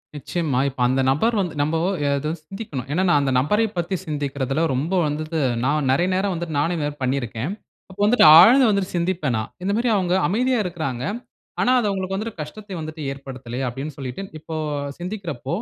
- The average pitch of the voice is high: No, medium, 160 Hz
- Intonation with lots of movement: Yes, wide, 5.7 semitones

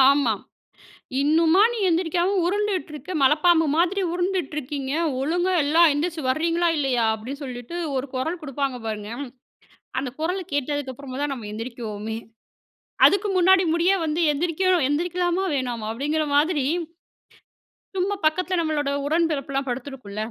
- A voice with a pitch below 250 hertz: No, very high, 300 Hz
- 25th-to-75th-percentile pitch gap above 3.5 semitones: Yes, average, 4.9 semitones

